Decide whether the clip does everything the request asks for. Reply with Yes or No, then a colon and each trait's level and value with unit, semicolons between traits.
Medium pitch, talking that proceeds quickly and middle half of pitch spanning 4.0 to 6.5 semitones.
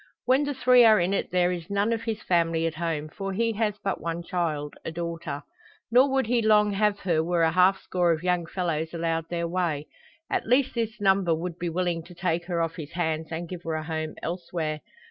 No: medium, 175 Hz; fast, 225 wpm; average, 3.6 semitones